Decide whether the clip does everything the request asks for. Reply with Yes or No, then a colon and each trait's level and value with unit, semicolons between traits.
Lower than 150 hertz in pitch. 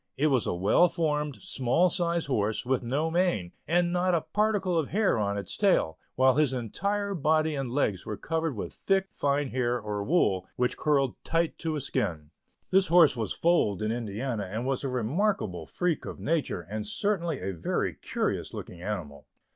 Yes: low, 135 Hz